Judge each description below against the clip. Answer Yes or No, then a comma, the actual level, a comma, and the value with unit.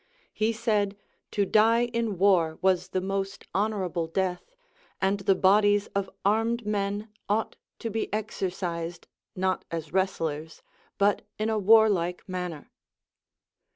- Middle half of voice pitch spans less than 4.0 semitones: Yes, average, 2.8 semitones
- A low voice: No, high, 195 Hz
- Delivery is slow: Yes, slow, 125 wpm